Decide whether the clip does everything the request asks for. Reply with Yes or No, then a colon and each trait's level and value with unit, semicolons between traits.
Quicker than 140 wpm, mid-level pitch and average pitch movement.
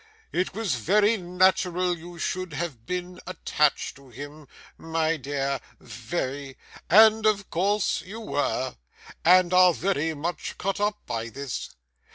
No: slow, 135 wpm; medium, 175 Hz; average, 4.5 semitones